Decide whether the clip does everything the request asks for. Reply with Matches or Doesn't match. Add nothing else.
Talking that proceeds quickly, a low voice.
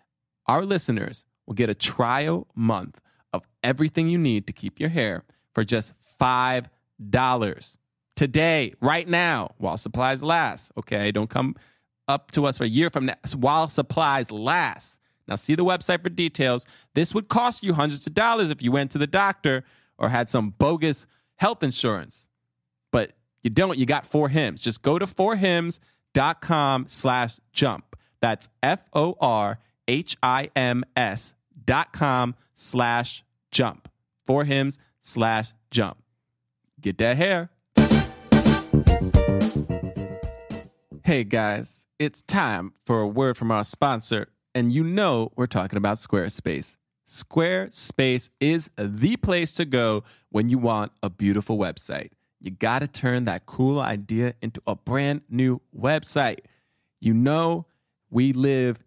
Doesn't match